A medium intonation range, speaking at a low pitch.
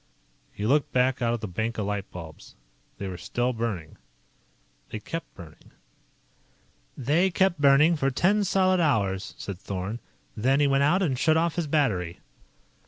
No: wide, 7.7 semitones; low, 125 Hz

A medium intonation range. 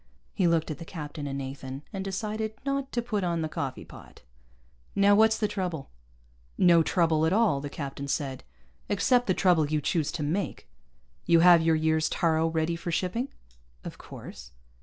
Yes: average, 4.6 semitones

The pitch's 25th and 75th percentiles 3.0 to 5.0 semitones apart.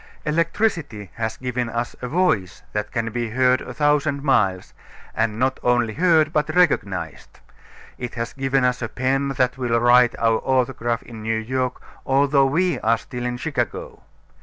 Yes: average, 3.3 semitones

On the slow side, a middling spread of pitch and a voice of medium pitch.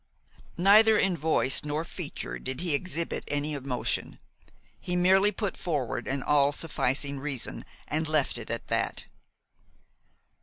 Yes: slow, 130 wpm; average, 4.3 semitones; medium, 150 Hz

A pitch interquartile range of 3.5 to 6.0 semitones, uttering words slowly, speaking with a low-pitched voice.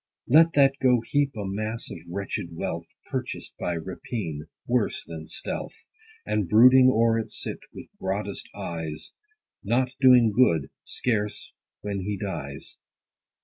Yes: average, 5.2 semitones; slow, 130 wpm; low, 105 Hz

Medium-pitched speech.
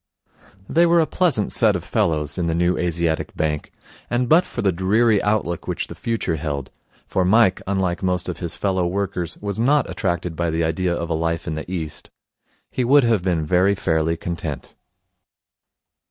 No: very low, 90 Hz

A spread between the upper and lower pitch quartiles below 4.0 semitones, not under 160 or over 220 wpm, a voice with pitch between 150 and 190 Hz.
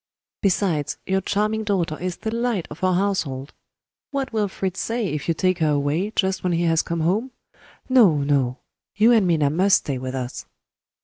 No: average, 5.3 semitones; average, 185 wpm; medium, 185 Hz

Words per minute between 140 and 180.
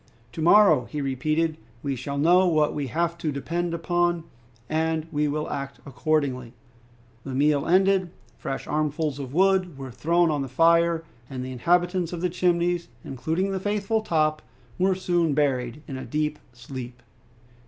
Yes: average, 160 wpm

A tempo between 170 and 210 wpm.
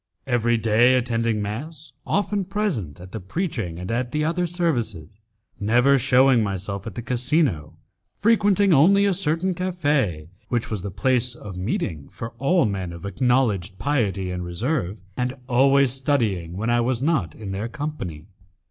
No: average, 155 wpm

